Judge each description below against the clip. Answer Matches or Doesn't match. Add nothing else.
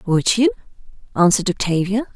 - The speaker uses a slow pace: Matches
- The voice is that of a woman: Matches